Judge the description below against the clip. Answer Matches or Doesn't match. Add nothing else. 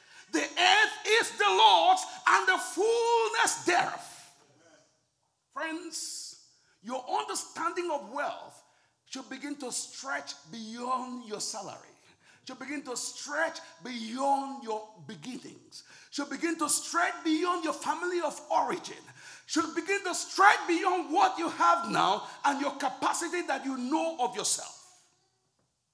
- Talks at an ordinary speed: Doesn't match